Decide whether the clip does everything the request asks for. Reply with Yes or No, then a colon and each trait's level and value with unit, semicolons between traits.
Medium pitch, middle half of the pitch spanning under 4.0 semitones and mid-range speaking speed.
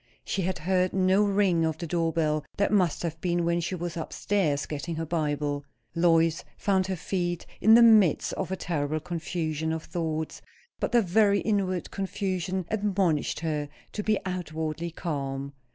Yes: medium, 170 Hz; average, 3.0 semitones; average, 170 wpm